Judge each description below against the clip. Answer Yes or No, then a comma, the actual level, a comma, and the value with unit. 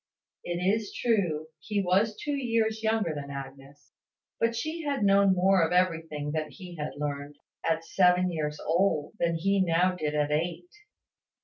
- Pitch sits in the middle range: Yes, medium, 180 Hz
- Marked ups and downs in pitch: No, average, 4.8 semitones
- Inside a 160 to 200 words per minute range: Yes, average, 165 wpm